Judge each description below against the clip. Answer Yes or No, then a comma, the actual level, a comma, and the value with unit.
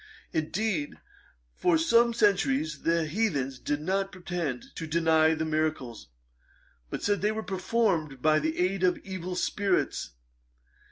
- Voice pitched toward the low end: No, medium, 165 Hz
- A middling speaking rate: No, slow, 130 wpm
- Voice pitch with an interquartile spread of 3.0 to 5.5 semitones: Yes, average, 4.1 semitones